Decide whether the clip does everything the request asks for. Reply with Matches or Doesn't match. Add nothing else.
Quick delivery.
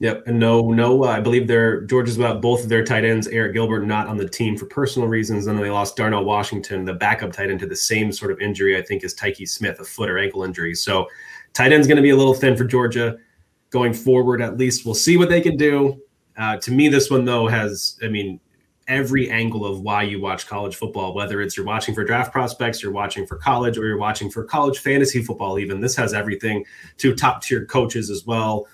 Matches